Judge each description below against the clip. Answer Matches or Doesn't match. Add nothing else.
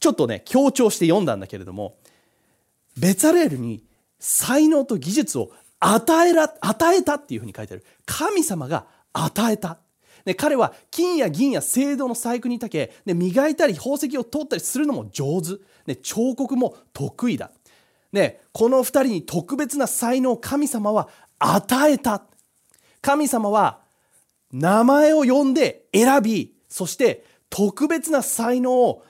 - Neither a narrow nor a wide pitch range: Doesn't match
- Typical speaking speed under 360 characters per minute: Matches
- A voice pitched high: Matches